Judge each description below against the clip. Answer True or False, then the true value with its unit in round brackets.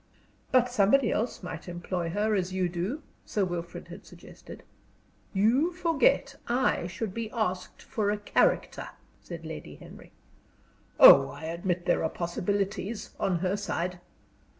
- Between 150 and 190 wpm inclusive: False (140 wpm)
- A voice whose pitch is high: True (195 Hz)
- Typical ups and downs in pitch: True (4.4 semitones)